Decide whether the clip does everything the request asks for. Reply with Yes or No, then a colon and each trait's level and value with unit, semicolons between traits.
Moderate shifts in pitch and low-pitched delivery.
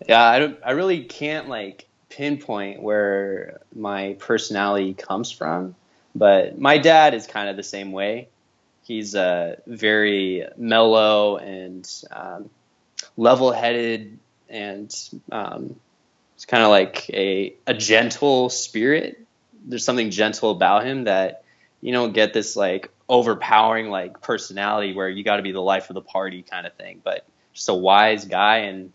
Yes: average, 3.2 semitones; low, 105 Hz